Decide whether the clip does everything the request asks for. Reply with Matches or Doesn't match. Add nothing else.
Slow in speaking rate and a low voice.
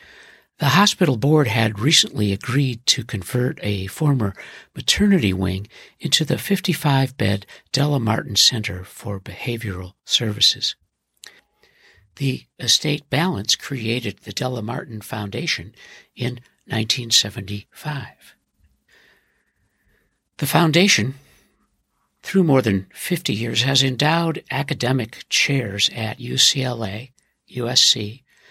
Matches